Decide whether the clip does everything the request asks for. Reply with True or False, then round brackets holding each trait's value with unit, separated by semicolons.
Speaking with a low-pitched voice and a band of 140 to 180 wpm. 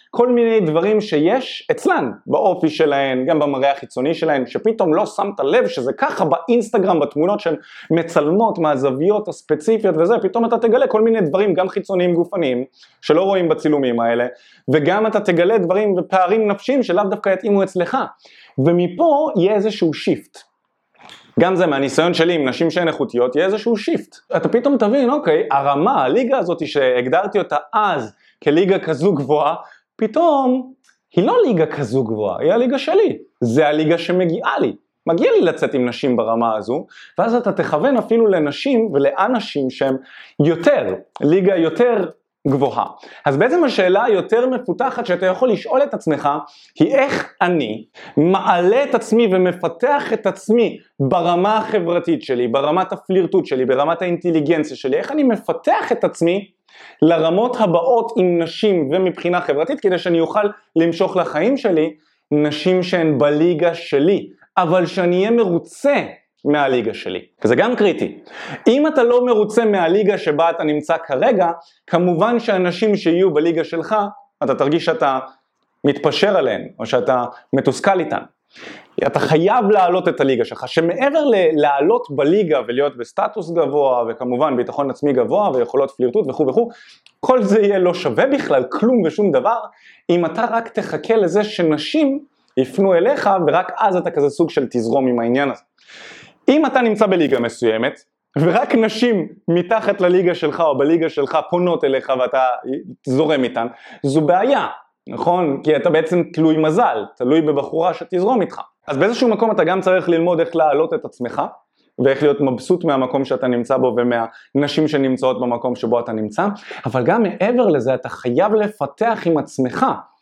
False (175 Hz; 150 wpm)